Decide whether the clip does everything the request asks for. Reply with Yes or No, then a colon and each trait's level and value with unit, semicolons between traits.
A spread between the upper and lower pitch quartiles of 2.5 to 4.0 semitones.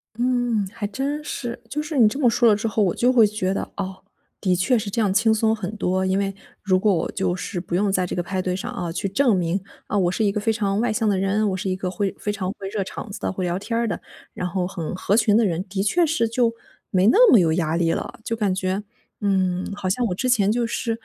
Yes: average, 3.5 semitones